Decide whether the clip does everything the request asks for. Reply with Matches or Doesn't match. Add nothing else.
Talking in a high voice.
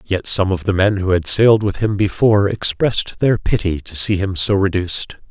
Doesn't match